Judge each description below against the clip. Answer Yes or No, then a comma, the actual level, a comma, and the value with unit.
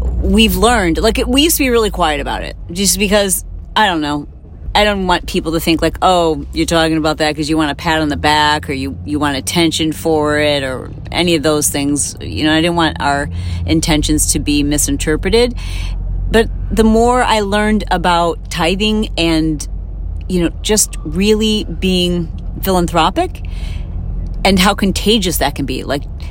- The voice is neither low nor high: Yes, medium, 160 Hz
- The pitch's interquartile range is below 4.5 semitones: No, average, 5.2 semitones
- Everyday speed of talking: Yes, average, 180 wpm